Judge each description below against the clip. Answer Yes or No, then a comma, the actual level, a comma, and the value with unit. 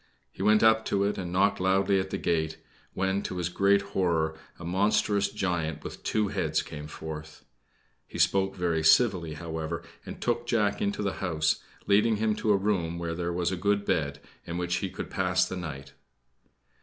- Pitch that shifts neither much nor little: Yes, average, 3.4 semitones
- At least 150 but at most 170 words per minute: No, average, 190 wpm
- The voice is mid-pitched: No, very low, 90 Hz